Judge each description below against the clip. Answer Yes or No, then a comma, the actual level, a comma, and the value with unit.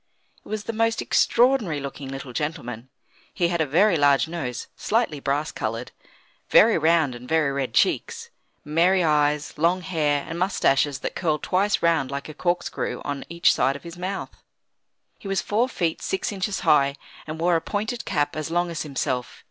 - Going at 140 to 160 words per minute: No, average, 180 wpm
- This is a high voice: No, medium, 160 Hz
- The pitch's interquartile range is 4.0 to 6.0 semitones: Yes, average, 4.7 semitones